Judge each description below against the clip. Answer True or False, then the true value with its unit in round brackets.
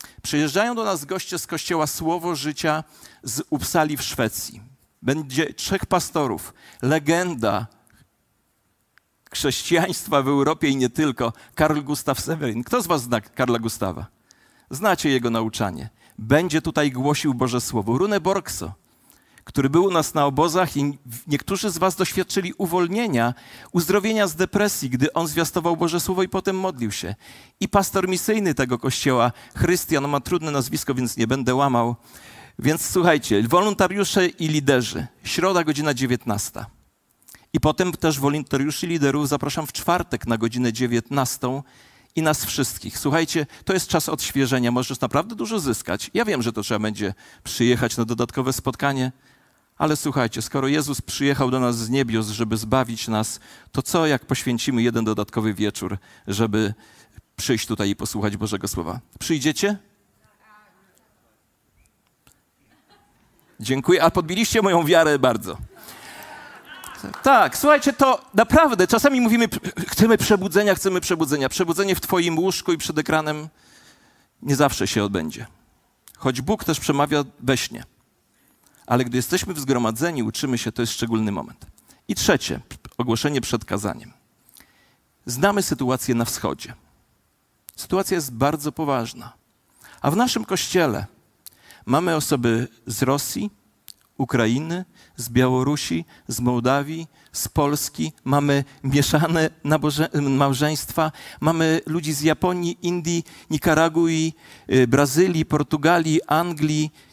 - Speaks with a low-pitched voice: False (145 Hz)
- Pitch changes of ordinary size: False (5.9 semitones)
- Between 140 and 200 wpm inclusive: False (130 wpm)